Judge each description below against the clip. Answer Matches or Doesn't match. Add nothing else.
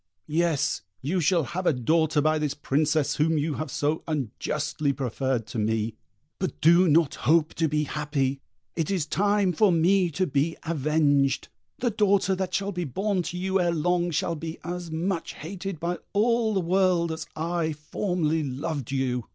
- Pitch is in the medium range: Matches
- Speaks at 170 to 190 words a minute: Matches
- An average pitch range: Matches